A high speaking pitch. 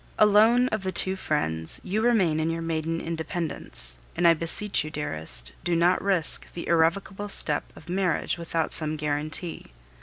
No: medium, 165 Hz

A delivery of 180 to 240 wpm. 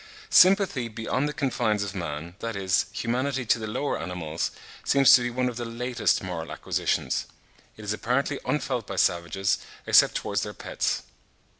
No: average, 165 wpm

